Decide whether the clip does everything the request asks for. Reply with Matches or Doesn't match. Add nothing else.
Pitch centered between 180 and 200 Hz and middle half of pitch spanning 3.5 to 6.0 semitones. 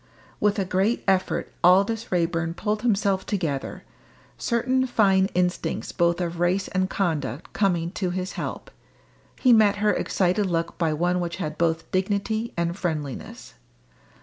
Doesn't match